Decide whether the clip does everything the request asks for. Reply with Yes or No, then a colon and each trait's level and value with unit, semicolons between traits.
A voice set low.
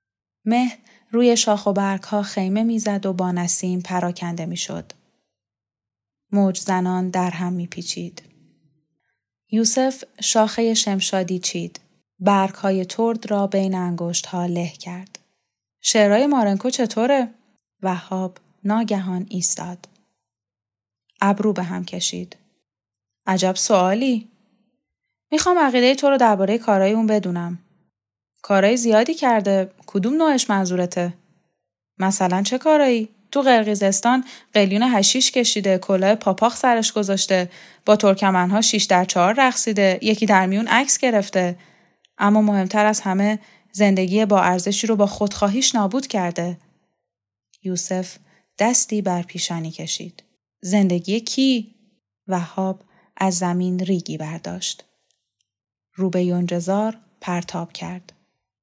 No: high, 195 Hz